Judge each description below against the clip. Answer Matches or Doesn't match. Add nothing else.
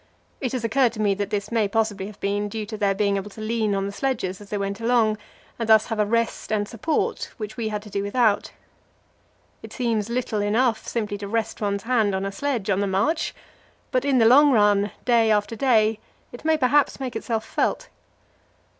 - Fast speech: Matches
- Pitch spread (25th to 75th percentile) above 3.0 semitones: Doesn't match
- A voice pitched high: Matches